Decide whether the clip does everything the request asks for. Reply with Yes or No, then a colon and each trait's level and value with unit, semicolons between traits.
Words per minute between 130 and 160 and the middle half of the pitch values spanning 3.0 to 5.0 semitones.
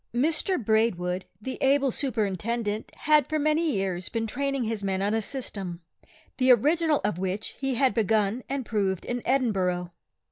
No: average, 155 wpm; wide, 5.5 semitones